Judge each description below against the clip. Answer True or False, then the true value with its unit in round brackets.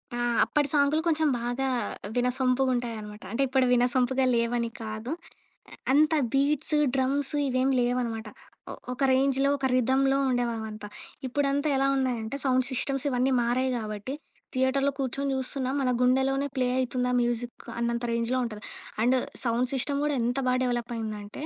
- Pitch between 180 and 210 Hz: False (255 Hz)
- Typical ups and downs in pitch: False (2.2 semitones)